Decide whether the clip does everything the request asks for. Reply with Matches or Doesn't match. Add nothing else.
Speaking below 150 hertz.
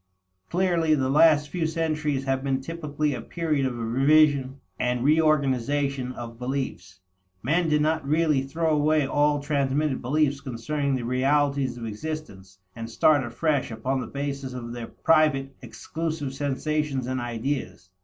Matches